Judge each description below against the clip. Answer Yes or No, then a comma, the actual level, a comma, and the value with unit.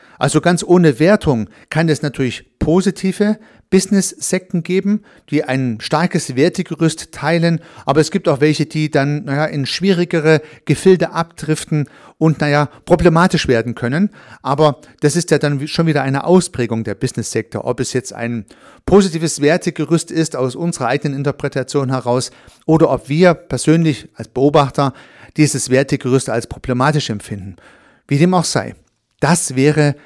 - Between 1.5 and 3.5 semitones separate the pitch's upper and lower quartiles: No, average, 4.1 semitones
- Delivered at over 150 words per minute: No, average, 145 wpm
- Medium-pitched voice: Yes, medium, 150 Hz